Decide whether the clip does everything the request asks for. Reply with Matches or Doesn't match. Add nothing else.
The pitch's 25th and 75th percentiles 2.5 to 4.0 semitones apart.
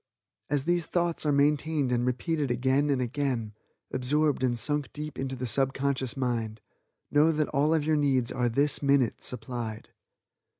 Matches